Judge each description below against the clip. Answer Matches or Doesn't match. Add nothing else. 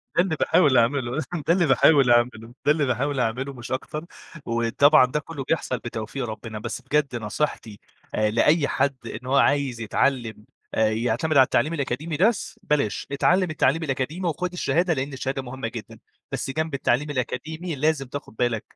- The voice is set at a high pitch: Doesn't match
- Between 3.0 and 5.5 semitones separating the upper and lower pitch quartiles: Matches